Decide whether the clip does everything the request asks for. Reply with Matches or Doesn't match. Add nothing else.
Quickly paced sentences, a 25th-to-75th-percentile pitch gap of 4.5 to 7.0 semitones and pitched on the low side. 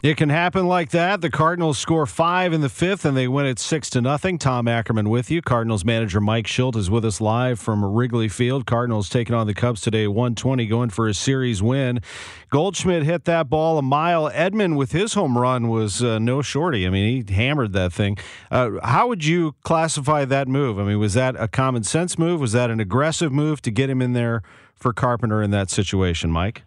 Matches